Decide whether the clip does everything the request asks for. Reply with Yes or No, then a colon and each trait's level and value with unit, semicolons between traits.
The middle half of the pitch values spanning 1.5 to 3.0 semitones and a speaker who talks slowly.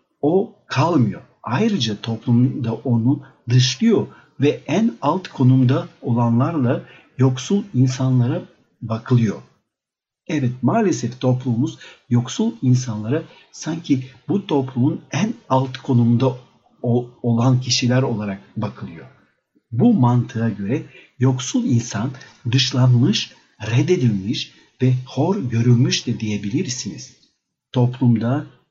Yes: narrow, 2.5 semitones; slow, 90 wpm